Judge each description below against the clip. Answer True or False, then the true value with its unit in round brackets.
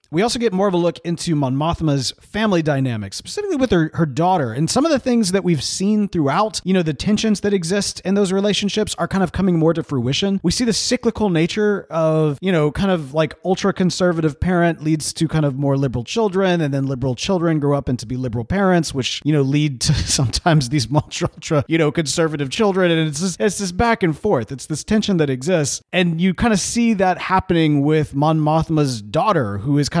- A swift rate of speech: True (220 wpm)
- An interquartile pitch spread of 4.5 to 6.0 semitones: True (4.8 semitones)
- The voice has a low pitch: False (170 Hz)